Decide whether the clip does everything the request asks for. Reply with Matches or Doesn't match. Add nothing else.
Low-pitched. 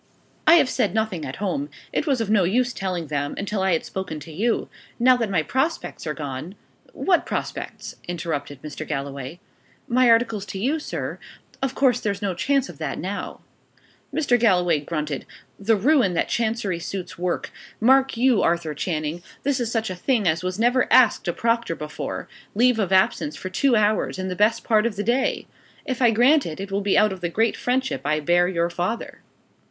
Doesn't match